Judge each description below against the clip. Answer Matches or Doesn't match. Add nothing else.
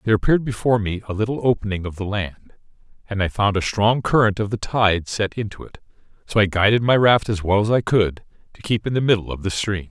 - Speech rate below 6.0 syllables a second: Doesn't match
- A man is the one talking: Matches